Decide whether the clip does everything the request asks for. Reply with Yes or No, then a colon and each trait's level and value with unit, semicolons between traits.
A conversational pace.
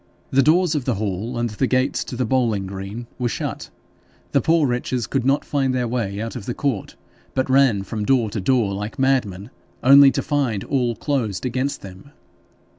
Yes: average, 190 wpm